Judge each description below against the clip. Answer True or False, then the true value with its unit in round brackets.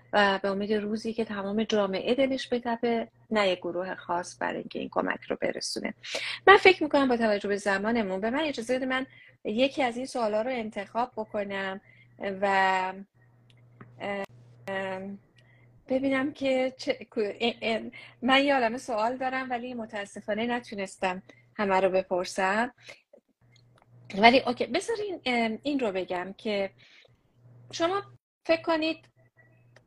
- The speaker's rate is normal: False (125 wpm)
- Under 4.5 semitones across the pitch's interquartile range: False (4.8 semitones)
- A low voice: False (215 Hz)